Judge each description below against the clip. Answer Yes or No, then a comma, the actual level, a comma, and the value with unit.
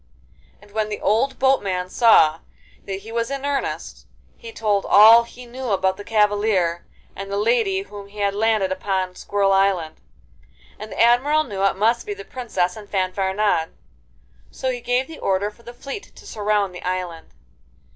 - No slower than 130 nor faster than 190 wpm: Yes, average, 175 wpm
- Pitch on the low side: No, high, 205 Hz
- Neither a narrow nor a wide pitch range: Yes, average, 3.7 semitones